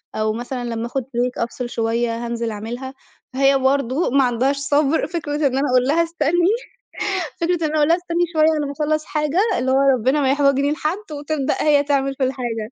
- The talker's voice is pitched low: No, very high, 275 Hz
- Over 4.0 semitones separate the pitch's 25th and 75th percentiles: No, average, 3.7 semitones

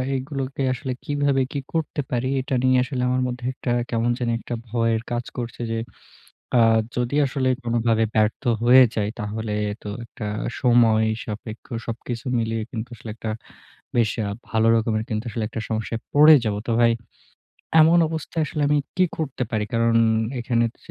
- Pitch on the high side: No, low, 120 Hz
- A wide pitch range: No, narrow, 2.6 semitones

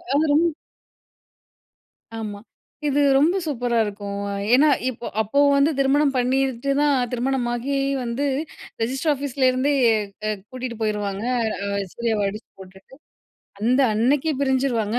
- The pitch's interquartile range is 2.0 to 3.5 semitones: No, average, 3.9 semitones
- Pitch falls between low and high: No, very high, 255 Hz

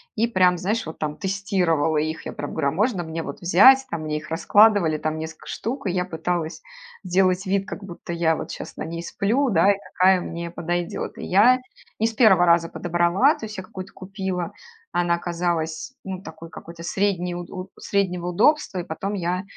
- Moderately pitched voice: Yes, medium, 180 Hz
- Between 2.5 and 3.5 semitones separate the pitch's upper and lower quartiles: Yes, average, 2.9 semitones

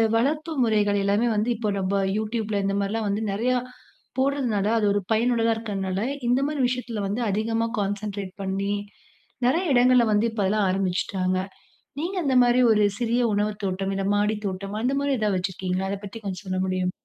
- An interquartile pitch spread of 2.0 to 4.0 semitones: Yes, average, 3.4 semitones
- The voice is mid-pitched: No, high, 210 Hz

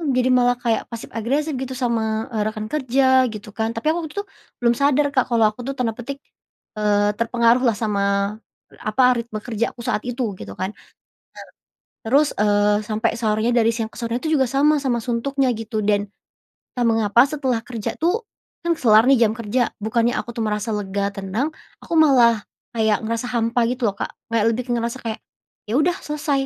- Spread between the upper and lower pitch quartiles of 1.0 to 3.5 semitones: Yes, average, 3.0 semitones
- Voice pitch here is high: Yes, high, 230 Hz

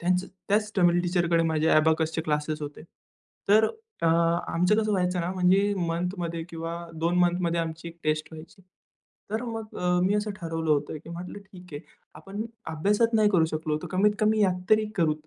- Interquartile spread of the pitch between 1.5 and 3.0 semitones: No, average, 3.6 semitones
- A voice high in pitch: No, medium, 175 Hz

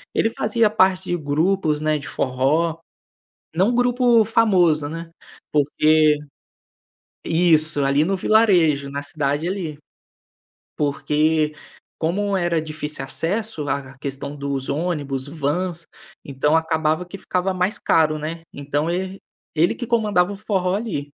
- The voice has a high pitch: No, medium, 160 Hz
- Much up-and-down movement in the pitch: No, average, 4.3 semitones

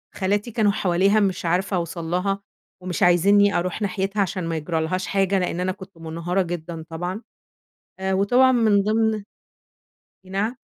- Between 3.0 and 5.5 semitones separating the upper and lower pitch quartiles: No, narrow, 2.5 semitones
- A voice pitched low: No, high, 190 Hz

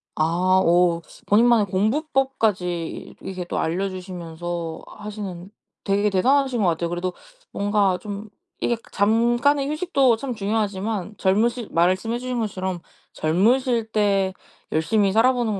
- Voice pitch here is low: No, high, 205 Hz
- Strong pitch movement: No, average, 4.3 semitones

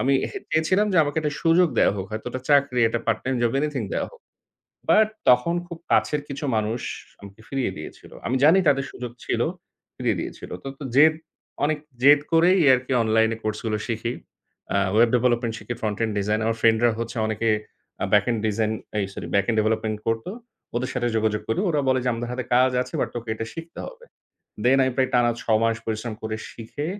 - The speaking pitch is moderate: No, low, 120 Hz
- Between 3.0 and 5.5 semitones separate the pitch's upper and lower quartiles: Yes, average, 4.2 semitones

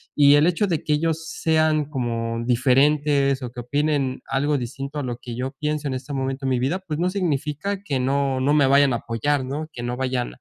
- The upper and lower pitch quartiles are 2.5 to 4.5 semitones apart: Yes, average, 2.8 semitones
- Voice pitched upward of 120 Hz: Yes, medium, 140 Hz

